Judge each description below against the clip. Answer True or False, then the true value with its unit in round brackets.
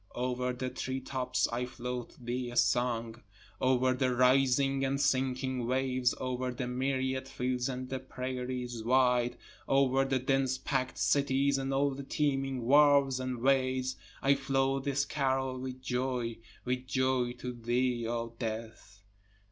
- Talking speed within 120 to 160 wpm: True (140 wpm)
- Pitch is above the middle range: False (130 Hz)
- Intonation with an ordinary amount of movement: False (1.3 semitones)